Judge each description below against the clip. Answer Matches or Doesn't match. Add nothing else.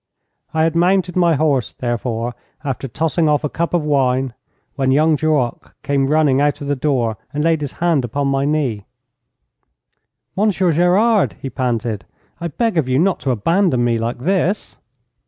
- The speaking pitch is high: Doesn't match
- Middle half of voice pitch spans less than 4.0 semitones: Doesn't match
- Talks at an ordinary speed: Matches